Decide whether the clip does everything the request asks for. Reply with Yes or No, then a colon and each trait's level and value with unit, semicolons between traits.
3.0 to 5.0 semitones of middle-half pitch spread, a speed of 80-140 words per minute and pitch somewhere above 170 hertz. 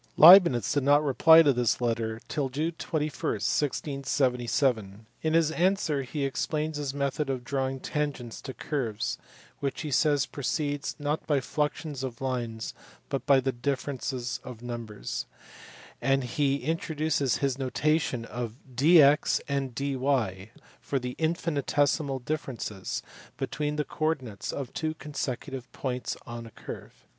No: average, 3.3 semitones; slow, 135 wpm; low, 135 Hz